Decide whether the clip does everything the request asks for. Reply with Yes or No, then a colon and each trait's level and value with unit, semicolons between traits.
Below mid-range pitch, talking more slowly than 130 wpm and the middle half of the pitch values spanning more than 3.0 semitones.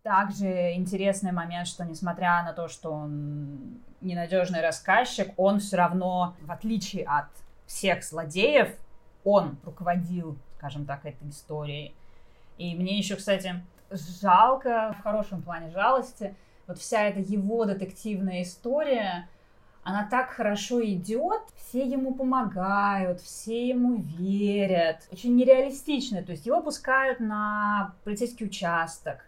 No: high, 190 Hz; average, 120 wpm; average, 3.9 semitones